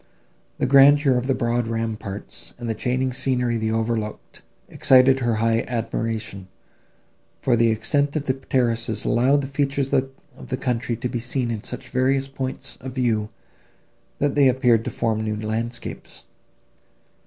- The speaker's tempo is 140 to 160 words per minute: Yes, average, 155 wpm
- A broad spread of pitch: No, average, 2.7 semitones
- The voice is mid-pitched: No, low, 125 Hz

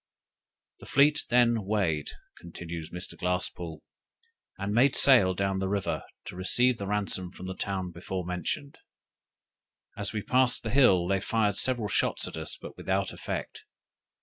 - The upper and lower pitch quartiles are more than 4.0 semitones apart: Yes, average, 4.4 semitones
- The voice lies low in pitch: Yes, low, 100 Hz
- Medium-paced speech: Yes, average, 150 wpm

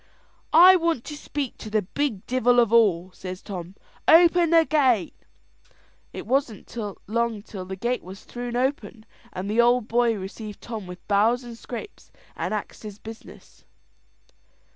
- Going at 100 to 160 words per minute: Yes, average, 155 wpm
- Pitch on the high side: Yes, high, 230 Hz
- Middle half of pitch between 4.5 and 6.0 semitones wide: No, average, 3.8 semitones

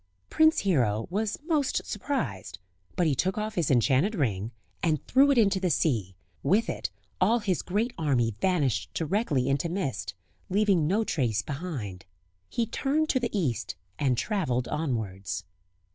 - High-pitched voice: No, medium, 165 Hz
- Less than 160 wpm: Yes, average, 150 wpm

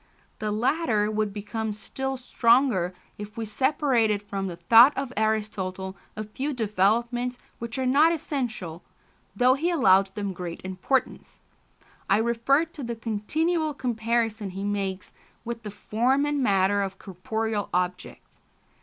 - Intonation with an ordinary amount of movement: Yes, average, 4.2 semitones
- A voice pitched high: Yes, high, 220 Hz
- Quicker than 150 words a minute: No, slow, 135 wpm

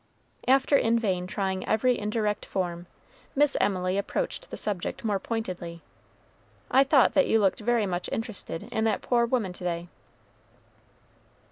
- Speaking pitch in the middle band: No, high, 210 Hz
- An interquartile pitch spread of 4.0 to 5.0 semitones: Yes, average, 4.5 semitones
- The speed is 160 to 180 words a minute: No, average, 145 wpm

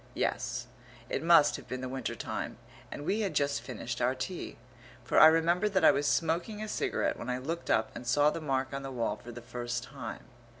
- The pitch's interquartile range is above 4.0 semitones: Yes, average, 4.8 semitones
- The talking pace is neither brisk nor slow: No, fast, 220 wpm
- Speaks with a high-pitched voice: No, medium, 140 Hz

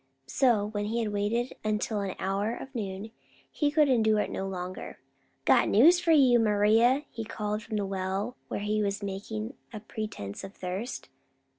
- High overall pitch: Yes, high, 215 Hz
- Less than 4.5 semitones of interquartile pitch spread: Yes, average, 2.8 semitones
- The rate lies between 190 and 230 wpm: No, average, 175 wpm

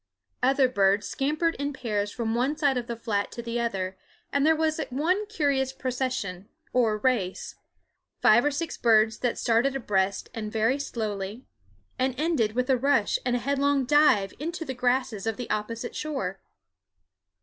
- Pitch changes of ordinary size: Yes, average, 4.5 semitones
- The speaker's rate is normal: Yes, average, 165 wpm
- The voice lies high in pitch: Yes, very high, 250 Hz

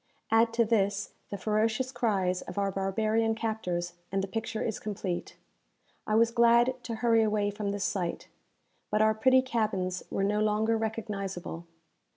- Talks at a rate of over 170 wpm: No, average, 160 wpm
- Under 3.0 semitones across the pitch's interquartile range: Yes, narrow, 2.5 semitones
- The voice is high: Yes, high, 215 Hz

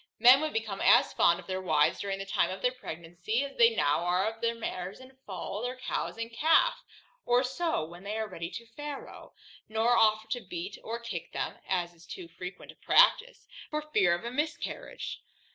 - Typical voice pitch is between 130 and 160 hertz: No, high, 220 Hz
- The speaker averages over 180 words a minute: Yes, fast, 205 wpm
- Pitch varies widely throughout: Yes, wide, 5.8 semitones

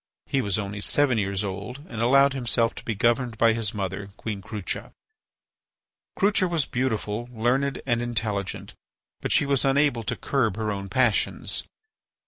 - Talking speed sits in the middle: Yes, average, 155 wpm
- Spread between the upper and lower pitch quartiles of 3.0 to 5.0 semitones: Yes, average, 4.1 semitones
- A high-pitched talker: No, low, 115 Hz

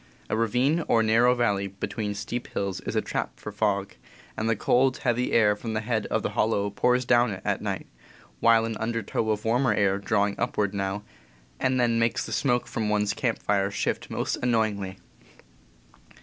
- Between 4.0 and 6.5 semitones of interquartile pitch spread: No, average, 2.7 semitones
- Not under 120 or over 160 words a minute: No, average, 185 wpm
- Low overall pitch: Yes, low, 110 Hz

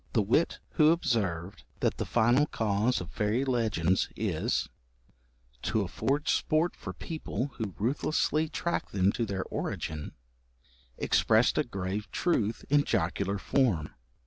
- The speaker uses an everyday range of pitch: No, wide, 6.3 semitones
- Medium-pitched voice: No, low, 110 Hz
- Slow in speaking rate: Yes, slow, 130 wpm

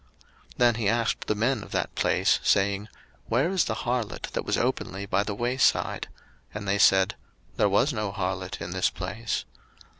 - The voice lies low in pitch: Yes, low, 105 Hz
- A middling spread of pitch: Yes, average, 3.3 semitones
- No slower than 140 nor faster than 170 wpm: No, average, 185 wpm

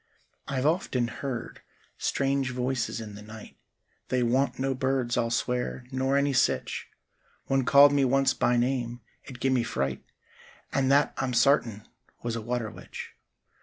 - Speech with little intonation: Yes, narrow, 2.3 semitones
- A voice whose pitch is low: Yes, low, 130 Hz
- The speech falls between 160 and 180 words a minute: No, average, 150 wpm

